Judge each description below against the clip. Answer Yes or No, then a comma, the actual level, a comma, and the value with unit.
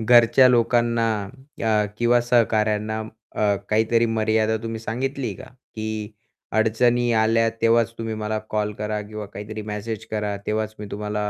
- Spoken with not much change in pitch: Yes, narrow, 1.5 semitones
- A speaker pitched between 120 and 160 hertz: No, low, 110 Hz